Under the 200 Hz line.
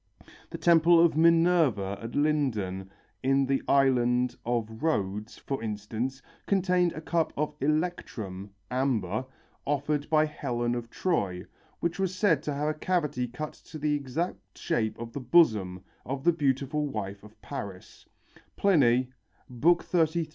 Yes: low, 135 Hz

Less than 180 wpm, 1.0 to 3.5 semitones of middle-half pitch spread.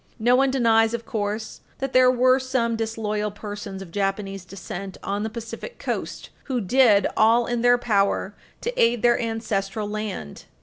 Yes: average, 165 wpm; average, 2.9 semitones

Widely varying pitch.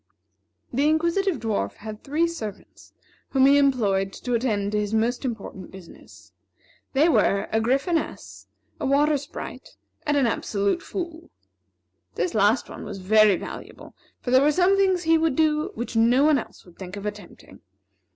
Yes: wide, 6.7 semitones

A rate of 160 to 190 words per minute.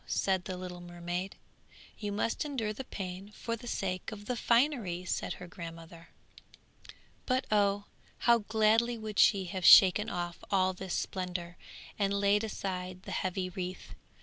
No: average, 150 wpm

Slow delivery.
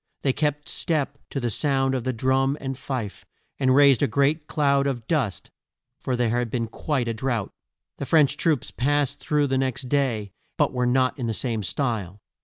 No: average, 190 wpm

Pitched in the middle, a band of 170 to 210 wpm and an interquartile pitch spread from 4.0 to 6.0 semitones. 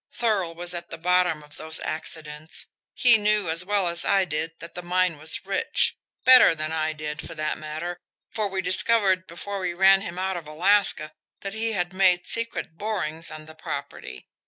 No: medium, 175 Hz; average, 190 wpm; average, 3.6 semitones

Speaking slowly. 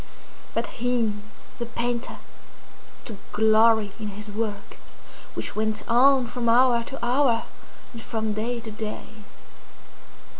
Yes: slow, 120 wpm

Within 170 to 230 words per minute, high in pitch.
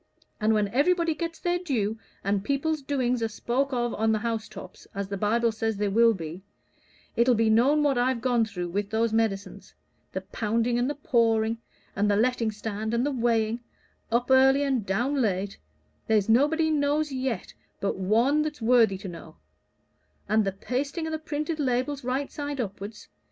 Yes: average, 180 wpm; high, 235 Hz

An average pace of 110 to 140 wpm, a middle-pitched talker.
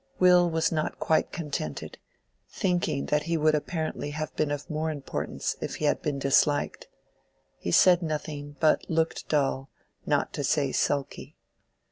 No: average, 150 wpm; medium, 155 Hz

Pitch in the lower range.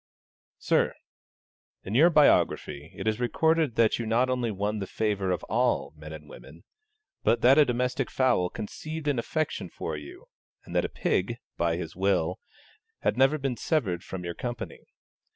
Yes: low, 115 Hz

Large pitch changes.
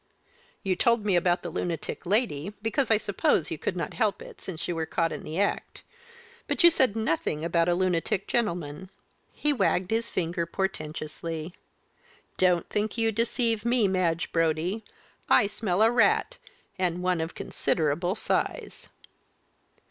No: average, 4.8 semitones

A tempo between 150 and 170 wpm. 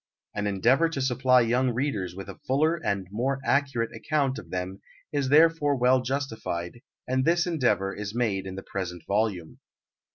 Yes: average, 165 wpm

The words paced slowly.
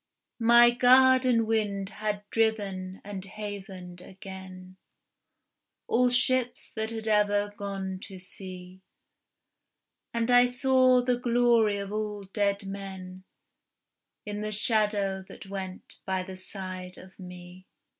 Yes: slow, 115 wpm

